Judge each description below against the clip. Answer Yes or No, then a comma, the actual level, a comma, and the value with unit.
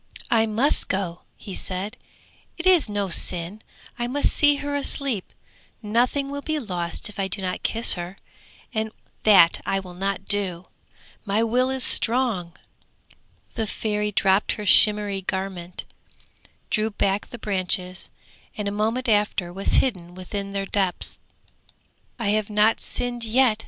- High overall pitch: Yes, high, 210 Hz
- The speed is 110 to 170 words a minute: Yes, average, 145 wpm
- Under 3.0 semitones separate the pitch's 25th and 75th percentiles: No, average, 3.4 semitones